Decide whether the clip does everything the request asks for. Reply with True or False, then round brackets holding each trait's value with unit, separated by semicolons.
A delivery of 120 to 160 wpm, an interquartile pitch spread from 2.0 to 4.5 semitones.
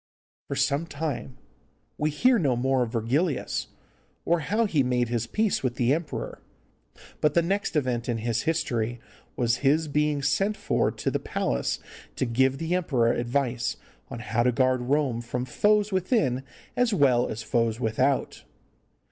False (155 wpm; 5.1 semitones)